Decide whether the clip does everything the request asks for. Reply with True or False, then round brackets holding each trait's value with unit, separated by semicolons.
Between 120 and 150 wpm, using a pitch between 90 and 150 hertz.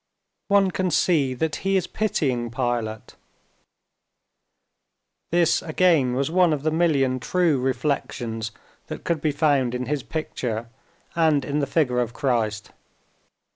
True (135 wpm; 140 Hz)